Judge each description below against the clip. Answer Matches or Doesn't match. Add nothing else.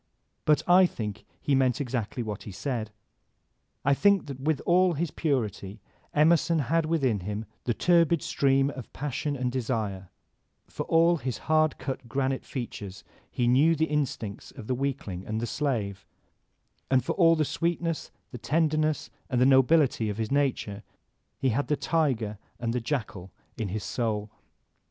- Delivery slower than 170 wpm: Matches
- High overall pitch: Doesn't match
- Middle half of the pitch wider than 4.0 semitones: Matches